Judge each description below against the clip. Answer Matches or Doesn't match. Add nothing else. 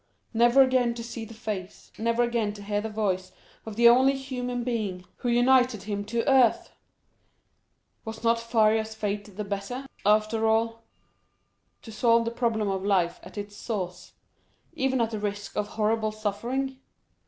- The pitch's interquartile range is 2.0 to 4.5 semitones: Matches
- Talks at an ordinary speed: Matches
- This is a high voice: Matches